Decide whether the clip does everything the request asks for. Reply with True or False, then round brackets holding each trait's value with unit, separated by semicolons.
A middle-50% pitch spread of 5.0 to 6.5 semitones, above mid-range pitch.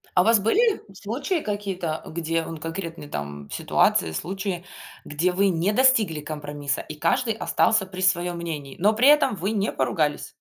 False (5.3 semitones; 180 Hz)